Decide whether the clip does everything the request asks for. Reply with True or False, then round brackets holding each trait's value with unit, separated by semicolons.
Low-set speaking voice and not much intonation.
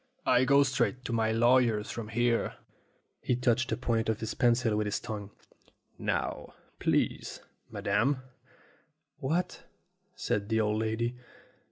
True (115 Hz; 2.3 semitones)